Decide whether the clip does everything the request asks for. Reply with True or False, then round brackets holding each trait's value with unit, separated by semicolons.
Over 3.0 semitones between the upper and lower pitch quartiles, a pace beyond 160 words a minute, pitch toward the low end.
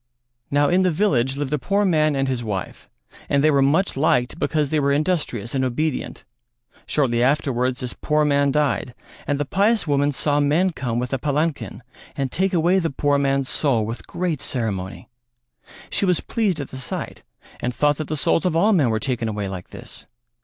False (3.6 semitones; 195 wpm; 145 Hz)